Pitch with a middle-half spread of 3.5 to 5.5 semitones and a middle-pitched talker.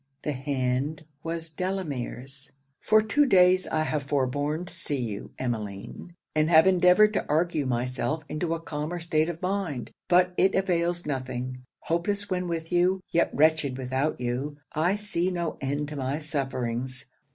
Yes: average, 4.8 semitones; medium, 155 Hz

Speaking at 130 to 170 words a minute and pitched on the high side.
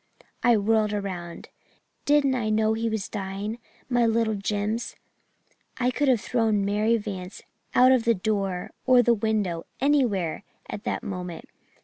Yes: average, 145 wpm; high, 215 Hz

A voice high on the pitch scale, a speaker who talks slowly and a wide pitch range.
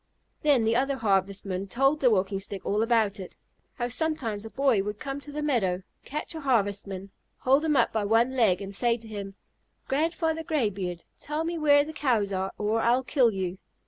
No: high, 230 Hz; average, 195 wpm; wide, 5.9 semitones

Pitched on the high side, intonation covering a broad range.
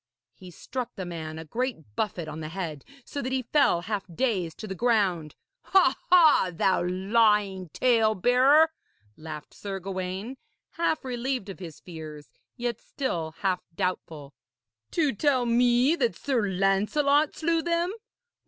Yes: high, 205 Hz; wide, 6.6 semitones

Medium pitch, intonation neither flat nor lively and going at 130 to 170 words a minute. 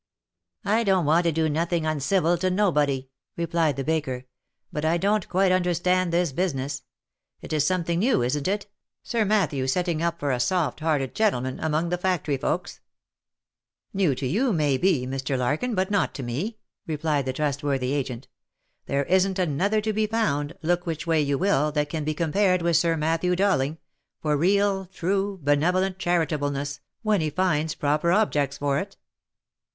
No: medium, 165 Hz; average, 4.4 semitones; average, 180 wpm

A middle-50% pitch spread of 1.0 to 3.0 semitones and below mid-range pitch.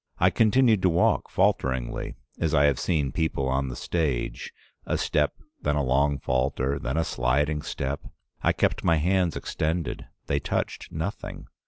No: average, 3.7 semitones; very low, 75 Hz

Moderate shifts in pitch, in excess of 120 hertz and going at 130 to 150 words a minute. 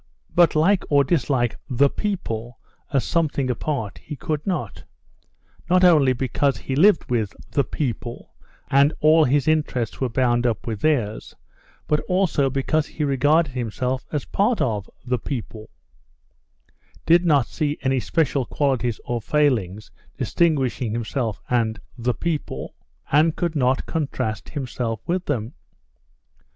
Yes: average, 4.4 semitones; low, 135 Hz; average, 140 wpm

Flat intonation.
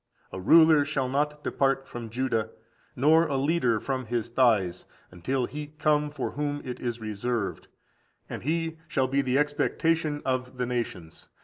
No: average, 3.7 semitones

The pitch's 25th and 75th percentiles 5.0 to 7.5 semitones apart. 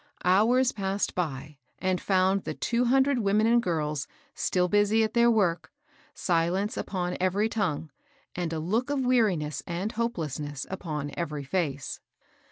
Yes: wide, 5.4 semitones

